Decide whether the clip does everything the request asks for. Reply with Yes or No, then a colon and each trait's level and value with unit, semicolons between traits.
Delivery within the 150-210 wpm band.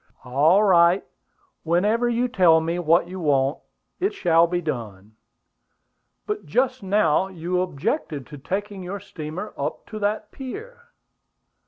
No: slow, 135 wpm